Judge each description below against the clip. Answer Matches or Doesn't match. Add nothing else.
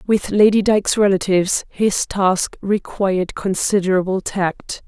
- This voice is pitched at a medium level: Doesn't match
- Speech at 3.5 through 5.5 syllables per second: Matches